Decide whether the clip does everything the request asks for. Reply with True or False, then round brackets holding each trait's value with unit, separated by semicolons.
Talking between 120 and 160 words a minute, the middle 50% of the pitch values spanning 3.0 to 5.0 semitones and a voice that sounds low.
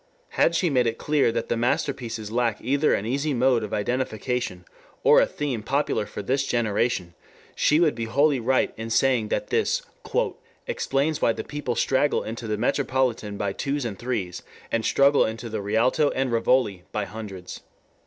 False (175 wpm; 3.7 semitones; 120 Hz)